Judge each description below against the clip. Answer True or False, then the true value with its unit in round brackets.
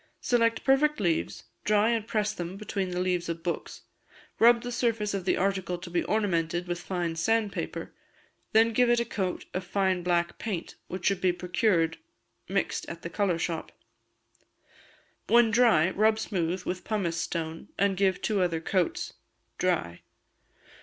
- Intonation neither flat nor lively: True (4.0 semitones)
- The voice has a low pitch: False (190 Hz)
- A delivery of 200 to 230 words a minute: False (160 wpm)